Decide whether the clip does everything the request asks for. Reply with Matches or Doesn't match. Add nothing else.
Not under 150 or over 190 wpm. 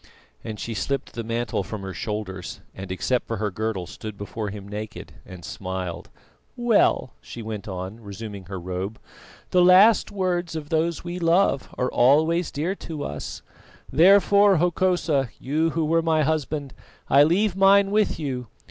Matches